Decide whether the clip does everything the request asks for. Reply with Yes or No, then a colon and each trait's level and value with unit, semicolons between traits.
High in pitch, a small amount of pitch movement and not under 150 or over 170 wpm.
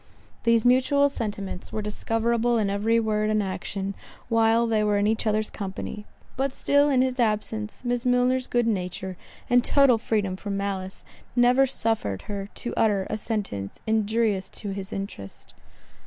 No: high, 220 Hz; average, 3.1 semitones; average, 155 wpm